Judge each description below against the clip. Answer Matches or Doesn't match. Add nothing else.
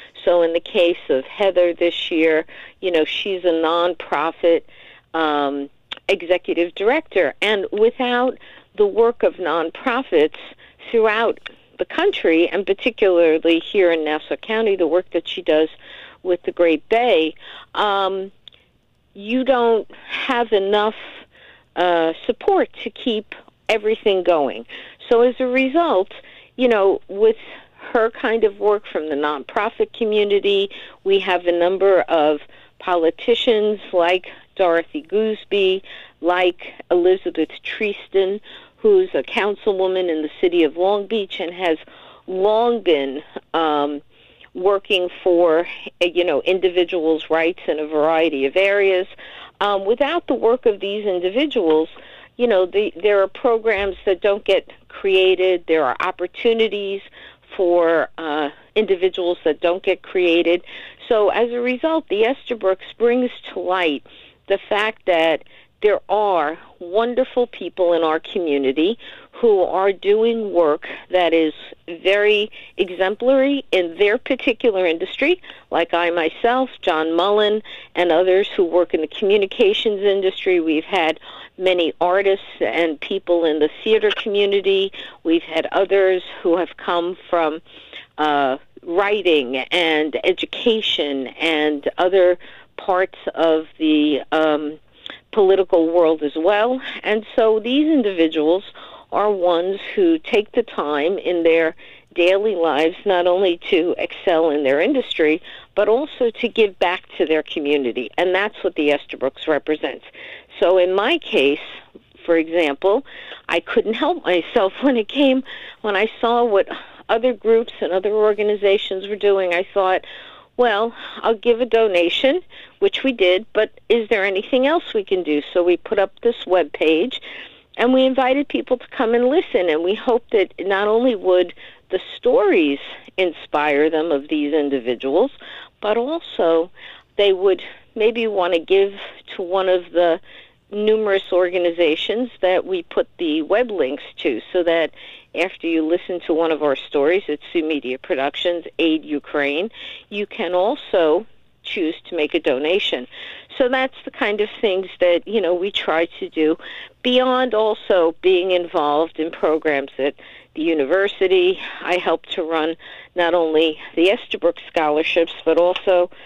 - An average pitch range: Doesn't match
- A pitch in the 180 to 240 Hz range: Matches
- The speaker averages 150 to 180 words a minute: Doesn't match